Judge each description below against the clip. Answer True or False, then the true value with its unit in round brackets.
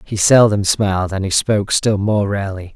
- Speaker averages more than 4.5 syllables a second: True (5.3 syllables/s)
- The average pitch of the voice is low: True (100 Hz)